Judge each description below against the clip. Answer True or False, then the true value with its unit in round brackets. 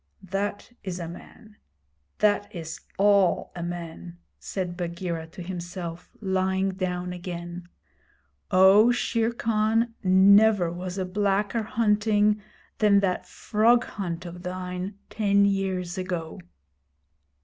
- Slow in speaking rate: True (115 wpm)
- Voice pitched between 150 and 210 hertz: True (190 Hz)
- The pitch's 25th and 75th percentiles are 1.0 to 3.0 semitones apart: True (2.7 semitones)